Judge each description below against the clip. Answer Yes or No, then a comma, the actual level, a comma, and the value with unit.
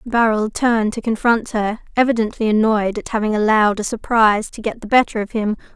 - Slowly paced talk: No, average, 190 wpm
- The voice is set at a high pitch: Yes, high, 220 Hz